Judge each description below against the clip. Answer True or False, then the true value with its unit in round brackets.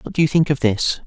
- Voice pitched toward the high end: False (140 Hz)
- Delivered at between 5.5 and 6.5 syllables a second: True (6.1 syllables/s)